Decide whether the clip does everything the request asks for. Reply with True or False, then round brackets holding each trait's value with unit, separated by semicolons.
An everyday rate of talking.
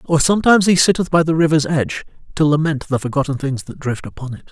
False (225 wpm)